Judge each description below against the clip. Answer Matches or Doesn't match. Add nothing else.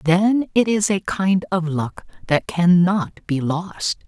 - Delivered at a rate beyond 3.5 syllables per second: Doesn't match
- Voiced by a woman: Matches